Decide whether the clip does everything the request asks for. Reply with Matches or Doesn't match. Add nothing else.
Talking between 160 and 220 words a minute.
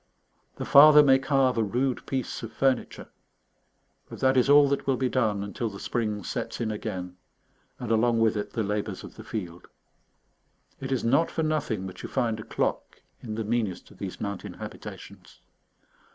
Matches